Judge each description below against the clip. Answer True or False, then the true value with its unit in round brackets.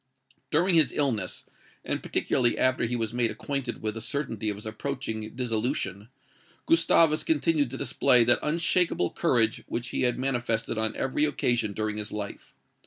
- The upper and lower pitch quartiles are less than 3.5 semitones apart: False (4.1 semitones)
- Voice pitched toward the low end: True (120 Hz)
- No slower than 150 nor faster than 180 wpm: True (160 wpm)